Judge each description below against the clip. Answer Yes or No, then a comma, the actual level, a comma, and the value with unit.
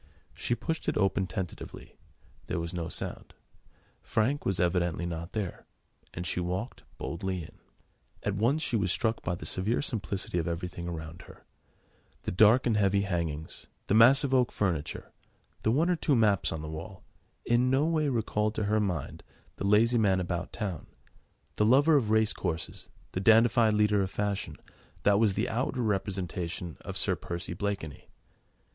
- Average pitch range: Yes, average, 4.4 semitones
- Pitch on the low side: Yes, low, 100 Hz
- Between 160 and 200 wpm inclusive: Yes, average, 165 wpm